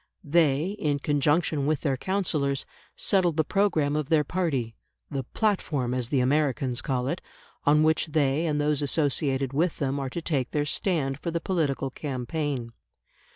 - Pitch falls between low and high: Yes, medium, 145 Hz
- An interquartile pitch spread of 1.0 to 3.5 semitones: Yes, average, 3.0 semitones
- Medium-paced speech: Yes, average, 160 wpm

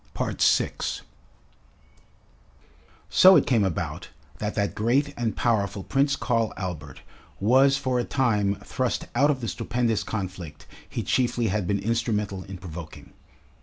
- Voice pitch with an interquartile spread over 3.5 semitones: Yes, average, 4.1 semitones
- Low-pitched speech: Yes, low, 110 Hz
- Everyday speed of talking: No, slow, 130 wpm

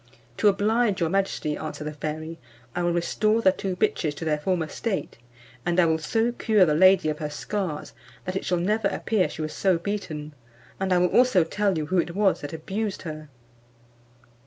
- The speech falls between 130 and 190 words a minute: No, average, 200 wpm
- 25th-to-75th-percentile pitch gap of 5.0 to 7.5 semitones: No, average, 4.3 semitones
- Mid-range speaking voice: Yes, medium, 180 Hz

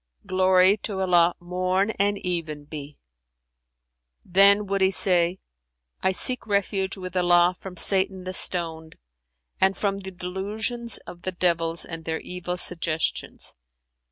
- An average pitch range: No, narrow, 2.0 semitones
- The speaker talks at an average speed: No, slow, 130 wpm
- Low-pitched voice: No, medium, 185 Hz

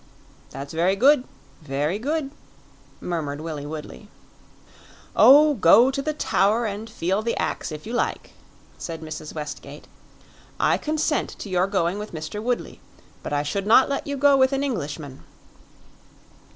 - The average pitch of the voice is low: No, high, 200 Hz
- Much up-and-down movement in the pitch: Yes, wide, 8.9 semitones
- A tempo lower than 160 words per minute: Yes, average, 150 wpm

